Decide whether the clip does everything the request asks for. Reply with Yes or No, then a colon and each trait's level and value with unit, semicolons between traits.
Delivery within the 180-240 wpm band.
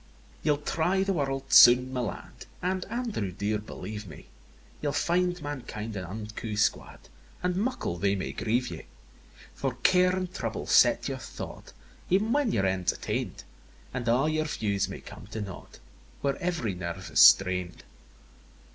No: average, 160 wpm